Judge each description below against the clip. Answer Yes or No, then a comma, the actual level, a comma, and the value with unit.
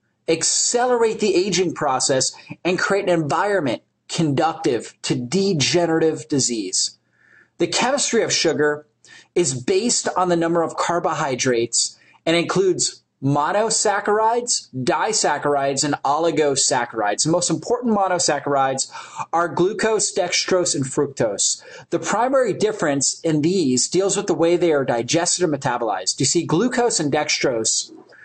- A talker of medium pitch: Yes, medium, 165 Hz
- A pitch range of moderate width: Yes, average, 4.7 semitones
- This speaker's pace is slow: Yes, slow, 120 wpm